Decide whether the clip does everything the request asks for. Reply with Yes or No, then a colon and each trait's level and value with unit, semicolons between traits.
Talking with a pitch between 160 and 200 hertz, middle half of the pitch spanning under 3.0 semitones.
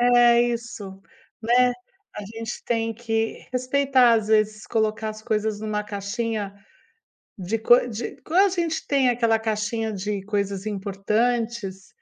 No: high, 225 Hz; narrow, 2.4 semitones